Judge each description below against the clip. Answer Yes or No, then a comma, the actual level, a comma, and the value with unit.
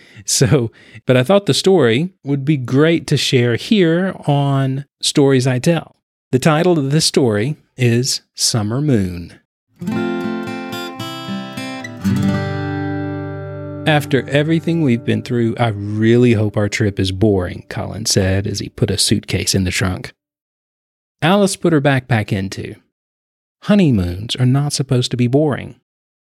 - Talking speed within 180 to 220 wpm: No, slow, 135 wpm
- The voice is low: Yes, low, 125 Hz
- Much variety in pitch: Yes, wide, 6.2 semitones